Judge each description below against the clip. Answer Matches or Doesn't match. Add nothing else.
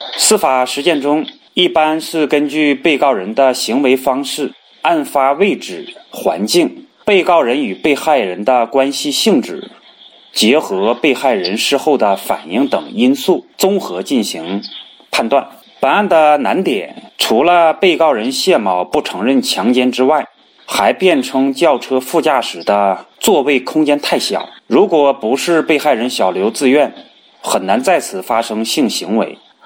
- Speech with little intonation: Doesn't match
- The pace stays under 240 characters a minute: Matches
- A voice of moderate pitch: Matches